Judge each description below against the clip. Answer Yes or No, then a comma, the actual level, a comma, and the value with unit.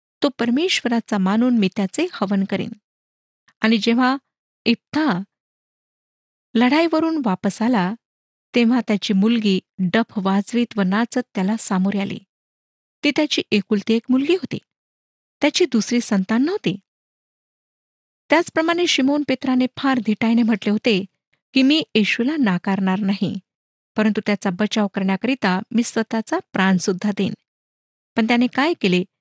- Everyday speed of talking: Yes, average, 115 wpm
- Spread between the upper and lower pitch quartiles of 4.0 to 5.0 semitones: Yes, average, 4.5 semitones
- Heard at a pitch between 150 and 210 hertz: No, high, 225 Hz